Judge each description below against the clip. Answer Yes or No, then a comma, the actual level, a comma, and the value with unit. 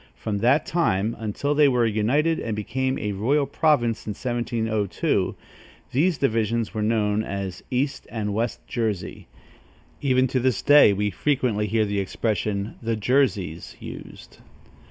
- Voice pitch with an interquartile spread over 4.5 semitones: No, average, 4.0 semitones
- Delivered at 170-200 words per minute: No, average, 140 wpm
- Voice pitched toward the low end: Yes, low, 115 Hz